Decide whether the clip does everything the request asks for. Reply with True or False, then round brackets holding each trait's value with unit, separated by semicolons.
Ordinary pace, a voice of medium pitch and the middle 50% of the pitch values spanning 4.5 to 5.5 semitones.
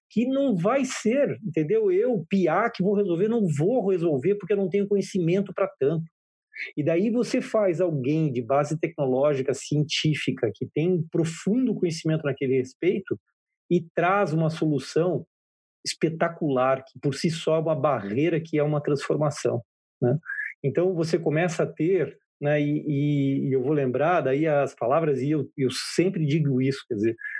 True (165 wpm; 160 Hz; 5.2 semitones)